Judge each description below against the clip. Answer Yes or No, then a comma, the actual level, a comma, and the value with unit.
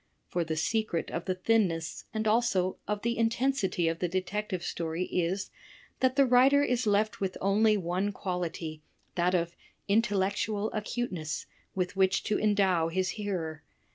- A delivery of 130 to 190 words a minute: Yes, average, 150 wpm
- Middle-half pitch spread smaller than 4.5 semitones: Yes, average, 3.6 semitones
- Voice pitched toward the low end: No, high, 195 Hz